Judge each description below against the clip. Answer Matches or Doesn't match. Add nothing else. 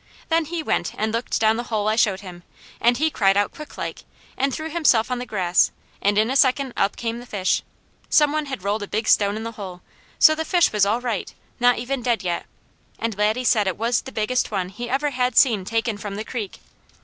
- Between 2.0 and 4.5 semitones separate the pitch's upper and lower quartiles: Matches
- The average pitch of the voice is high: Matches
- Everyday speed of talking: Doesn't match